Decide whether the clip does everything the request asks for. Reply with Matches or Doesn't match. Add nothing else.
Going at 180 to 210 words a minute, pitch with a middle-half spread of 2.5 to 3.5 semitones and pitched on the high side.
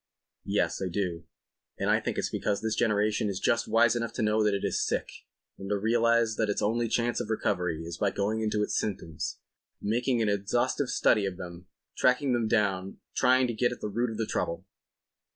Doesn't match